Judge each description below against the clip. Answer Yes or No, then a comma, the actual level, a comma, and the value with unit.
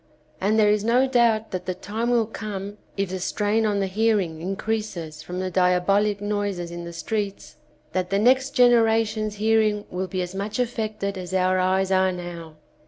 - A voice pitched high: Yes, high, 200 Hz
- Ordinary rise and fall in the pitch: Yes, average, 3.0 semitones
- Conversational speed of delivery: Yes, average, 190 wpm